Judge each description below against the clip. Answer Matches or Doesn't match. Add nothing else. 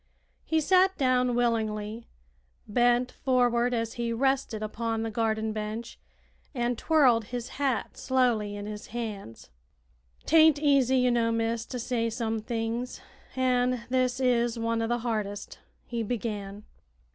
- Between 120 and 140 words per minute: Matches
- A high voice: Matches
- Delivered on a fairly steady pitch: Matches